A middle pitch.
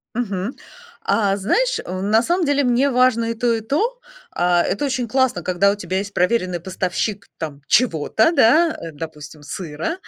No: high, 210 Hz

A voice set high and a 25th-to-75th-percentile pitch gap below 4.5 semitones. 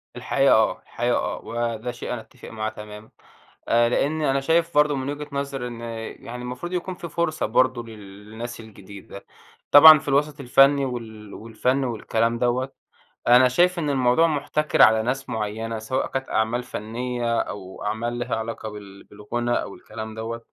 No: low, 120 Hz; average, 3.8 semitones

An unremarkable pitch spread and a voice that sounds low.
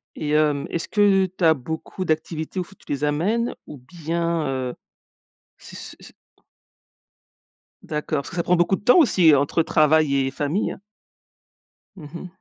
No: average, 3.4 semitones; medium, 160 Hz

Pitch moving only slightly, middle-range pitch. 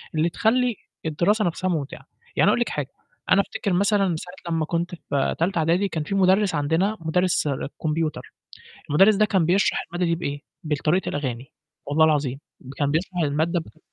No: average, 3.8 semitones; medium, 170 Hz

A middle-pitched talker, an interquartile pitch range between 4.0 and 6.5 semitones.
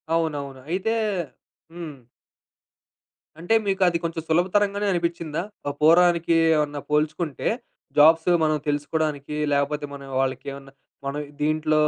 No: medium, 155 Hz; narrow, 2.6 semitones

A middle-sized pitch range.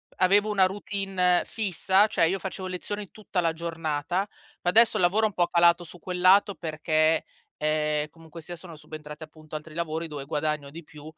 Yes: average, 3.3 semitones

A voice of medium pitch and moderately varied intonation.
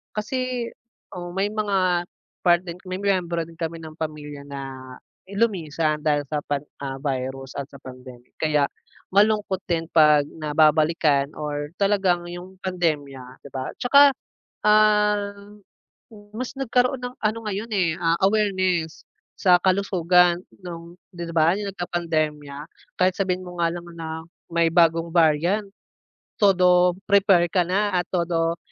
Yes: medium, 175 Hz; average, 3.9 semitones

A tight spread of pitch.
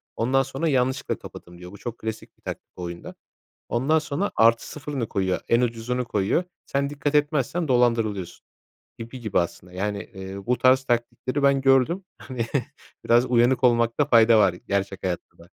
No: average, 4.6 semitones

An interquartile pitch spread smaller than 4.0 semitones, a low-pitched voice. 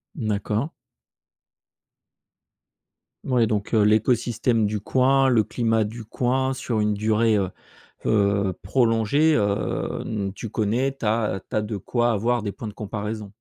Yes: narrow, 2.5 semitones; low, 110 Hz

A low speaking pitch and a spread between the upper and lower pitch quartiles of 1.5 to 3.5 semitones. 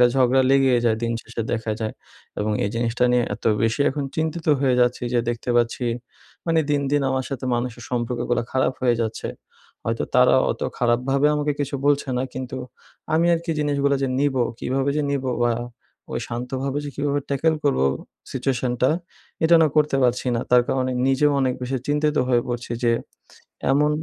Yes: low, 130 Hz; average, 2.8 semitones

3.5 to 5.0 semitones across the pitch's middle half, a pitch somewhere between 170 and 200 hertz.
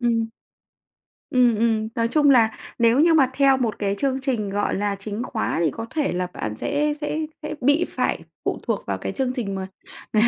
No: average, 4.5 semitones; high, 235 Hz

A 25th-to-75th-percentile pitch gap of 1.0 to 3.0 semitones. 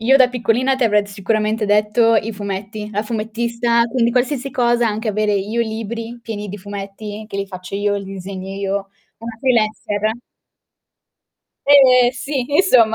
Yes: narrow, 2.6 semitones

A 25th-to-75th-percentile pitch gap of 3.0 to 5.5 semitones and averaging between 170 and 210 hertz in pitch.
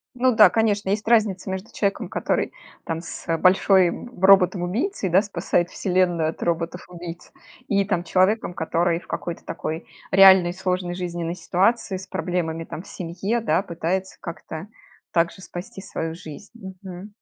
No: narrow, 2.4 semitones; medium, 185 Hz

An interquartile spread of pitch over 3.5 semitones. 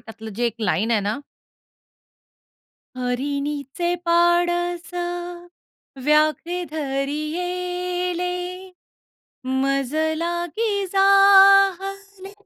Yes: average, 4.4 semitones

